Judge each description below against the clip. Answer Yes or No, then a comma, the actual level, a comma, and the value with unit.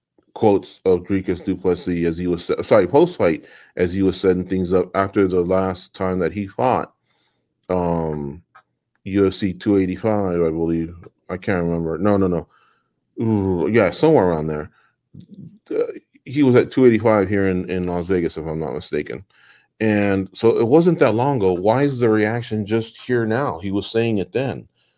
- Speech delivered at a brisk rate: No, average, 175 wpm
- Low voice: Yes, very low, 95 Hz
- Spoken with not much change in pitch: No, average, 3.9 semitones